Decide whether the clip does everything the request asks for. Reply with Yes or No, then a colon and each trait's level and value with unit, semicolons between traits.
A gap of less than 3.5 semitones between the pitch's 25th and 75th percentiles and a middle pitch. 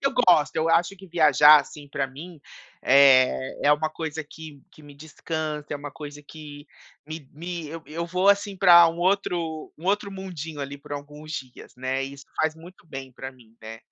Yes: average, 3.1 semitones; medium, 155 Hz